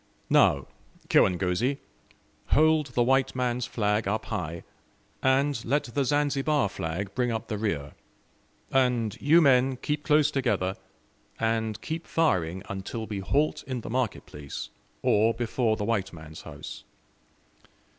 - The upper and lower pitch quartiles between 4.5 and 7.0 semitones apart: Yes, average, 5.2 semitones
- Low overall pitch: Yes, low, 120 Hz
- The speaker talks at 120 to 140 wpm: Yes, slow, 135 wpm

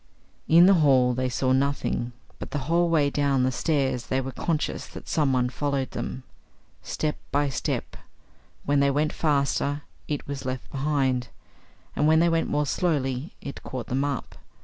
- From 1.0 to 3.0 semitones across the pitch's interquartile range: Yes, narrow, 2.5 semitones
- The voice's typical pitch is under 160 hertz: Yes, medium, 140 Hz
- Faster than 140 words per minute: Yes, average, 170 wpm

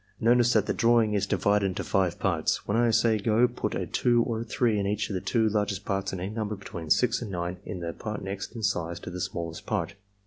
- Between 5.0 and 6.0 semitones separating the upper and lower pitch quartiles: No, average, 3.2 semitones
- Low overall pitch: Yes, low, 105 Hz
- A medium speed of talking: No, fast, 250 wpm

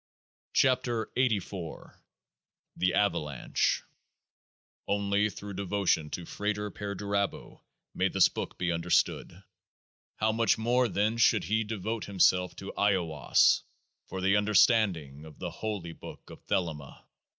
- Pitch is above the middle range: No, low, 100 Hz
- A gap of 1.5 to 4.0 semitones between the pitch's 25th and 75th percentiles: Yes, average, 3.3 semitones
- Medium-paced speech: No, slow, 130 wpm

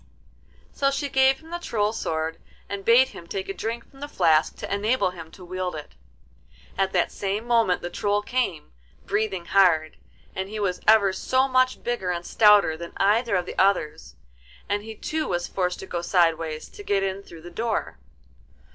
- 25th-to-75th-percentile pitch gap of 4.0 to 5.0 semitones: Yes, average, 4.7 semitones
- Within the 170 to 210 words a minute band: Yes, average, 190 wpm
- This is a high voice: Yes, high, 195 Hz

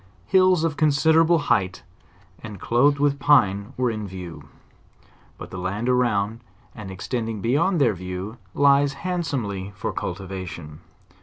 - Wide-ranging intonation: Yes, wide, 6.9 semitones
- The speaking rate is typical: No, slow, 130 wpm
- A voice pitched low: Yes, low, 115 Hz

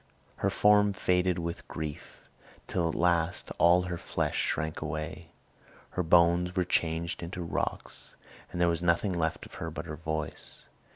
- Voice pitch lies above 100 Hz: No, very low, 85 Hz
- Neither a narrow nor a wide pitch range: No, narrow, 1.6 semitones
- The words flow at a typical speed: Yes, average, 160 wpm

